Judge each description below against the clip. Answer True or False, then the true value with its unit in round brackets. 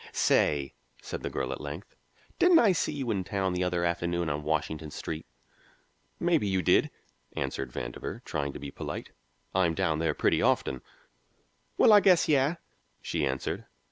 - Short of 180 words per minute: True (165 wpm)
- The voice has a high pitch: False (85 Hz)